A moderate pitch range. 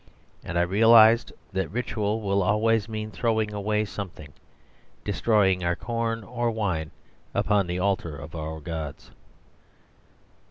Yes: average, 4.2 semitones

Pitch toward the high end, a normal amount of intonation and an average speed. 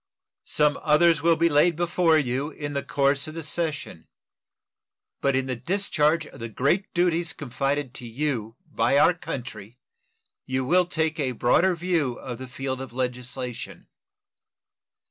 No: medium, 145 Hz; average, 4.4 semitones; average, 150 wpm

